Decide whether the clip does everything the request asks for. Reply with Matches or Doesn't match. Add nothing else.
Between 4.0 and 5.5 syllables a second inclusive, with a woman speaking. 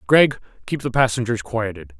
Doesn't match